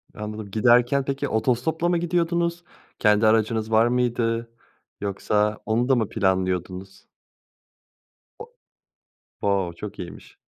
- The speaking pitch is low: Yes, low, 110 Hz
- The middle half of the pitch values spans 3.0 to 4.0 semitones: Yes, average, 3.6 semitones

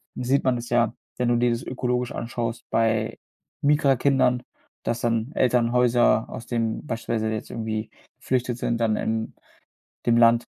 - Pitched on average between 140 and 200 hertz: No, low, 120 Hz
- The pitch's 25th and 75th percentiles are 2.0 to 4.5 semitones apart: No, narrow, 1.5 semitones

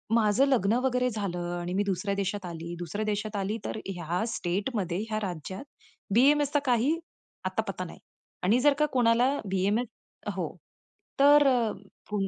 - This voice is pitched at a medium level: No, high, 210 Hz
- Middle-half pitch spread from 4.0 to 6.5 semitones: Yes, average, 4.9 semitones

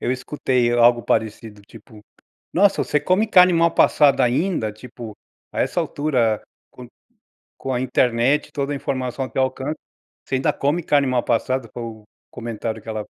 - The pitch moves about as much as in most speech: Yes, average, 3.8 semitones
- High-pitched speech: No, low, 125 Hz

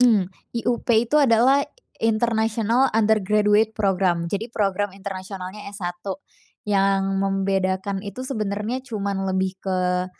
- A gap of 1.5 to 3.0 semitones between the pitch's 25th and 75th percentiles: Yes, narrow, 2.5 semitones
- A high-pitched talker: Yes, high, 200 Hz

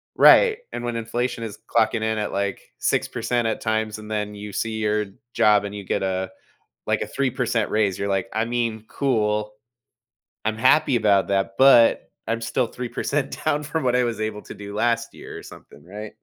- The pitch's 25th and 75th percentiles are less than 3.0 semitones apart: Yes, narrow, 2.5 semitones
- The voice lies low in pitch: Yes, low, 110 Hz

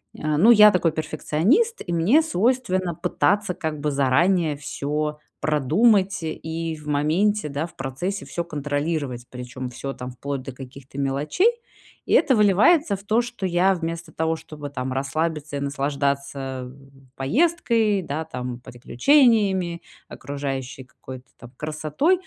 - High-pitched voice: No, medium, 155 Hz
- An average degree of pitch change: No, wide, 5.8 semitones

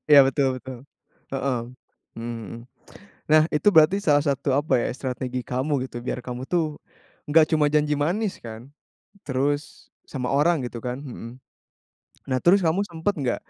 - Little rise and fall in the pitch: No, average, 3.3 semitones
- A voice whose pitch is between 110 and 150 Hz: Yes, medium, 140 Hz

